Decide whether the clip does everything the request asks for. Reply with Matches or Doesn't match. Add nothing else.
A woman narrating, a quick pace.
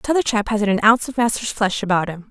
Matches